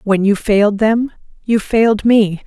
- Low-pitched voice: No, high, 210 Hz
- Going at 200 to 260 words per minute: No, average, 170 wpm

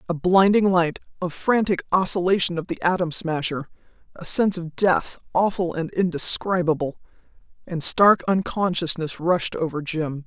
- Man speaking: No, female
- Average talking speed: No, slow, 130 wpm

